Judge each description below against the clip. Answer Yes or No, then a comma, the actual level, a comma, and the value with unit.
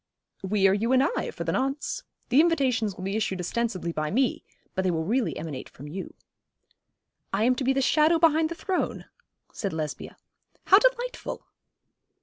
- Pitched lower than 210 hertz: No, high, 235 Hz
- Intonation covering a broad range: Yes, wide, 7.7 semitones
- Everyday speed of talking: Yes, average, 175 wpm